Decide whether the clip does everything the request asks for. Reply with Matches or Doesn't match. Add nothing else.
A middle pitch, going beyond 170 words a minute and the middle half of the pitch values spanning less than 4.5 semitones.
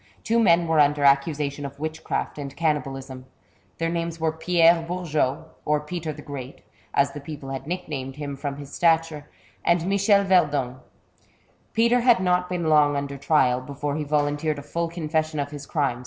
Matches